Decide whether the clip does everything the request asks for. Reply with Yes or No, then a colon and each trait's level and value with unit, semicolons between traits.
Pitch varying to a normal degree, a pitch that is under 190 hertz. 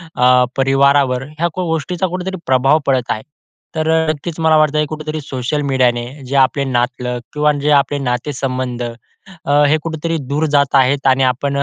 Yes: average, 3.1 semitones; medium, 140 Hz